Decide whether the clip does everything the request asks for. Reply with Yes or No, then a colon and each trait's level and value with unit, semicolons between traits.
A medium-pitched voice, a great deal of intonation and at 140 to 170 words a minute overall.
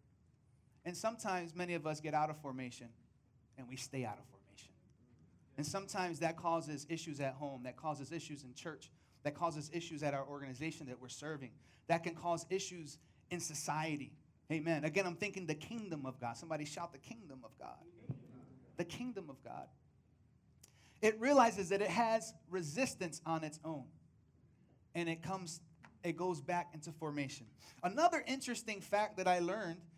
No: medium, 160 Hz; average, 4.2 semitones; average, 165 wpm